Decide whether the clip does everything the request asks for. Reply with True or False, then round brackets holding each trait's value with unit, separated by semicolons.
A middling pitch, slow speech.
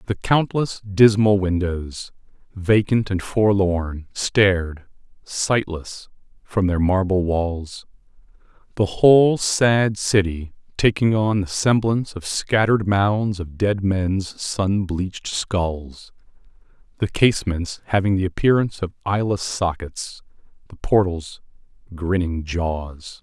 False (95 Hz; 105 wpm)